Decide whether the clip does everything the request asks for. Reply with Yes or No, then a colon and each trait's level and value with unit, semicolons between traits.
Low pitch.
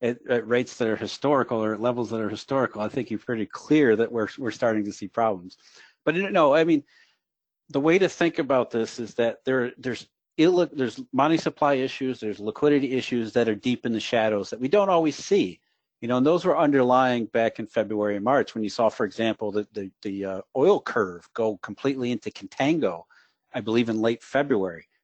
Yes: low, 120 Hz